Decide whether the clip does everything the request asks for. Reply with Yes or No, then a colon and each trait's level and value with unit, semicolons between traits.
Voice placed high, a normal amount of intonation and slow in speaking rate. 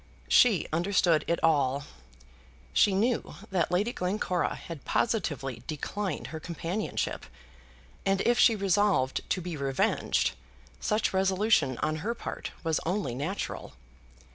No: medium, 180 Hz; average, 4.7 semitones; slow, 120 wpm